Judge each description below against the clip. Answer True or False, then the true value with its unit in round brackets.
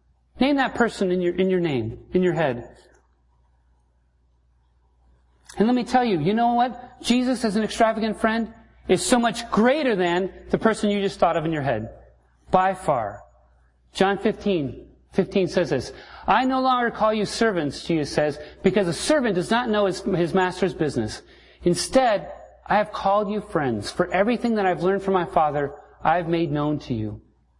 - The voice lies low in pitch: False (185 Hz)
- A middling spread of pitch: False (7.8 semitones)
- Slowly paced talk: False (180 wpm)